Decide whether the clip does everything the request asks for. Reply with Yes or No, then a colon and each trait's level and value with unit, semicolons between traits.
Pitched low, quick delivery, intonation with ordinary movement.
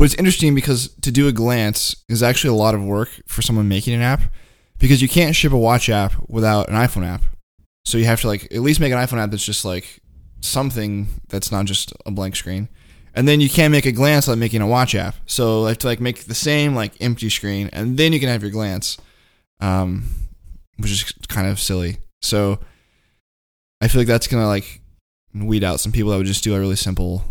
Yes: low, 105 Hz; fast, 230 wpm; average, 4.1 semitones